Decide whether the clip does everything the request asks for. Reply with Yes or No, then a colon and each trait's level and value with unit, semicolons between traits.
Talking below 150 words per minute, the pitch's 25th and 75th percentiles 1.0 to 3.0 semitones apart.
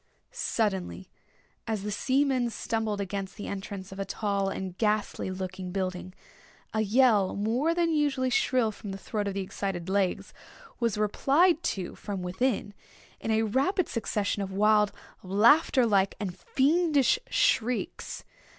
No: average, 140 wpm; average, 4.6 semitones